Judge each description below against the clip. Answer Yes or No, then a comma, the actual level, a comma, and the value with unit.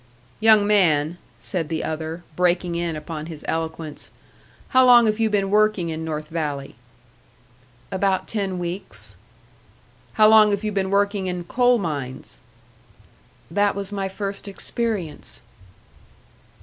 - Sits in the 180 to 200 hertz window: Yes, high, 190 Hz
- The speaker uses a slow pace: Yes, slow, 130 wpm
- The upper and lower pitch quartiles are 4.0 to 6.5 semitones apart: Yes, average, 4.3 semitones